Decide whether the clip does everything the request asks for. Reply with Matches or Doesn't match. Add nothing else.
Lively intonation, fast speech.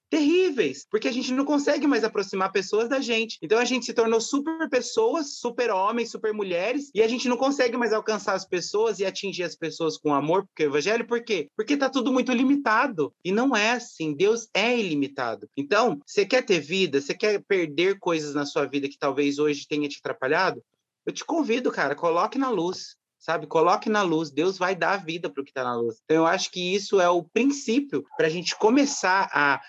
Matches